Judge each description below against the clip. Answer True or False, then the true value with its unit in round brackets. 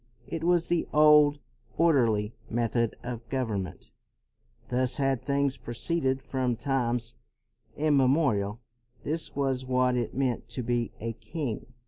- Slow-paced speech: True (120 wpm)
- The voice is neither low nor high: False (130 Hz)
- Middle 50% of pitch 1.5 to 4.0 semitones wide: True (3.3 semitones)